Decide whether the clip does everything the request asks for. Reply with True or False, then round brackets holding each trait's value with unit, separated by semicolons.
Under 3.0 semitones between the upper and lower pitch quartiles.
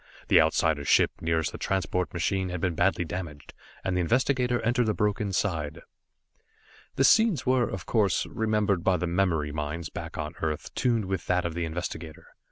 False (4.5 semitones)